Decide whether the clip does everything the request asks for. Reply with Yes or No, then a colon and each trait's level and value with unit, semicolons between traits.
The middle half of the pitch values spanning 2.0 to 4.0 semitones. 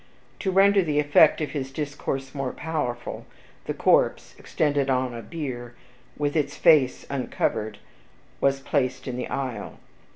Yes: average, 2.8 semitones